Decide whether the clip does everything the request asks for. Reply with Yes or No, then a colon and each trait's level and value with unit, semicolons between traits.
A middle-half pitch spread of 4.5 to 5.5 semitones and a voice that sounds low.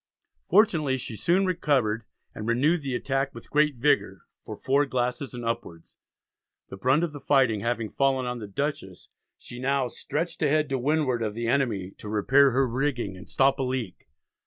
No: average, 3.6 semitones; low, 130 Hz